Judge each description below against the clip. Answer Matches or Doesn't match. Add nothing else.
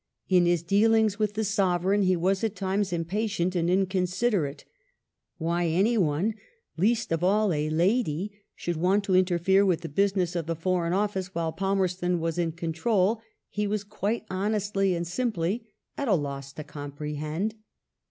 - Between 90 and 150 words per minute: Doesn't match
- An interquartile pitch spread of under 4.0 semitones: Matches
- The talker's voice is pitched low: Doesn't match